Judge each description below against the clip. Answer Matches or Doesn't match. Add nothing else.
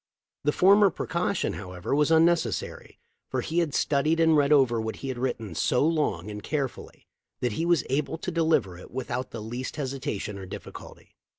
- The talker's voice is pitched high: Doesn't match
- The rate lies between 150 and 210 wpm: Matches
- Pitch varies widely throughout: Matches